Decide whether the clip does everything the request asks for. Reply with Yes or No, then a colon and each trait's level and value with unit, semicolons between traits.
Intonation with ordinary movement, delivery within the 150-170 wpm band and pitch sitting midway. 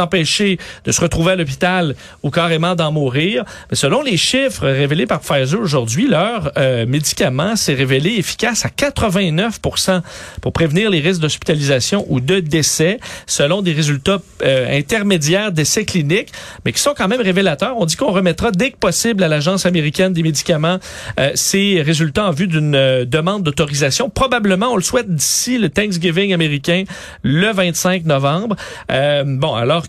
Yes: average, 4.7 semitones; average, 165 wpm; medium, 175 Hz